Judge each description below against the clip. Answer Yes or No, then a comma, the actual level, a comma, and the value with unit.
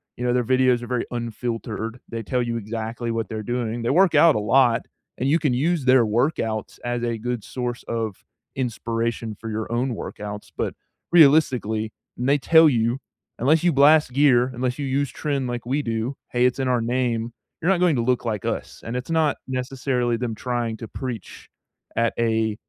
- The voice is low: Yes, low, 120 Hz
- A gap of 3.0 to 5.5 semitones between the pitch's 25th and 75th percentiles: No, narrow, 2.6 semitones